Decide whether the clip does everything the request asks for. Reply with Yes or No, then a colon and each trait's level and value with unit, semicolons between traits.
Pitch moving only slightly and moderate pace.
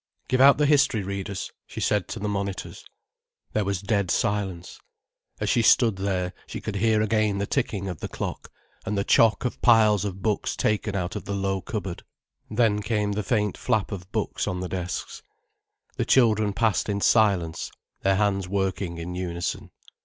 Yes: narrow, 2.1 semitones; average, 180 wpm